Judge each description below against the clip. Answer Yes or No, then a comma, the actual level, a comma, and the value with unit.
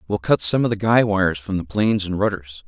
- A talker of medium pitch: No, low, 100 Hz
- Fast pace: Yes, fast, 270 wpm